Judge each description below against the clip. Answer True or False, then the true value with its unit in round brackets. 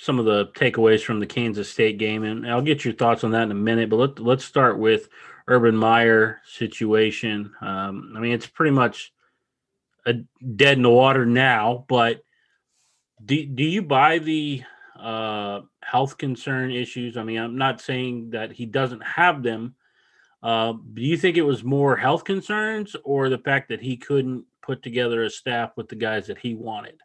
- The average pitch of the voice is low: True (120 Hz)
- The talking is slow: False (185 wpm)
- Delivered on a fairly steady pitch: False (3.2 semitones)